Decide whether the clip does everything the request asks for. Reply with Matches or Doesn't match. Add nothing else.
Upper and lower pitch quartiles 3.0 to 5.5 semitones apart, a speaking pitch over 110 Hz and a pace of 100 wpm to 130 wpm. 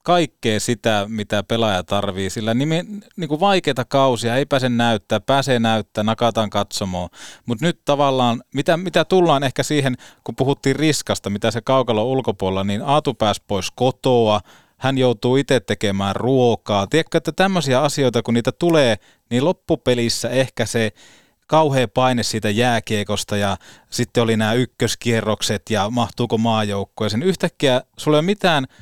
Doesn't match